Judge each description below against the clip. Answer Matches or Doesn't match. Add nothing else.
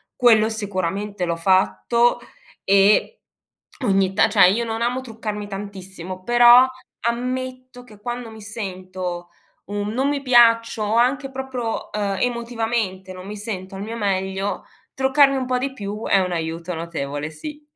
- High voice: Matches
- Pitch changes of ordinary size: Matches